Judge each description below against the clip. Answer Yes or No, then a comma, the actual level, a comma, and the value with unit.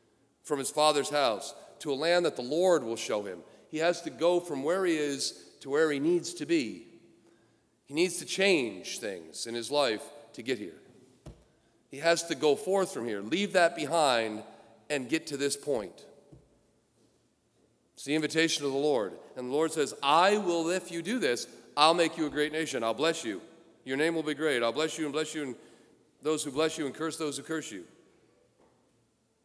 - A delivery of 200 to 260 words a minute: Yes, fast, 205 wpm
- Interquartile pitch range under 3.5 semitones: Yes, average, 2.8 semitones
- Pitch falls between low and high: Yes, medium, 155 Hz